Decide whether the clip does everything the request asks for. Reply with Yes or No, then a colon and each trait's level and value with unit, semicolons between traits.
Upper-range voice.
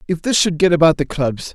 No: medium, 165 Hz